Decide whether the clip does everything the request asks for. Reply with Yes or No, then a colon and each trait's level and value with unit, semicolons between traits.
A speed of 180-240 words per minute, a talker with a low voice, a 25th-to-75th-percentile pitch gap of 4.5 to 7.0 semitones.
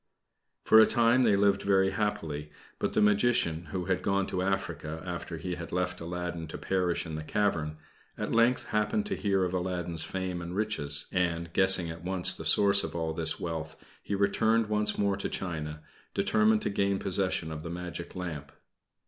No: average, 185 wpm; very low, 90 Hz; average, 3.3 semitones